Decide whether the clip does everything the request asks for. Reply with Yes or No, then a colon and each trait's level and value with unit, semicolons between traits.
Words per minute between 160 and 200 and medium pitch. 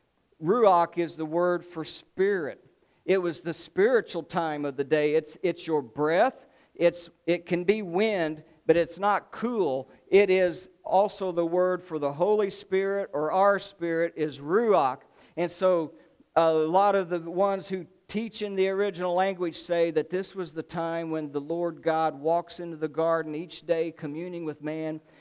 Yes: average, 175 wpm; medium, 170 Hz